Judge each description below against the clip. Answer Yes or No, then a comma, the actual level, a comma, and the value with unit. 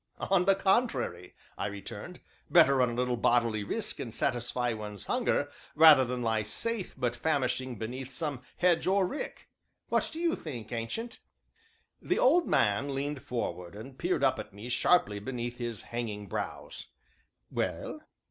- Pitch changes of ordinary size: No, wide, 7.0 semitones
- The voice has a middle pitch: No, low, 125 Hz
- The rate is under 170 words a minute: Yes, average, 155 wpm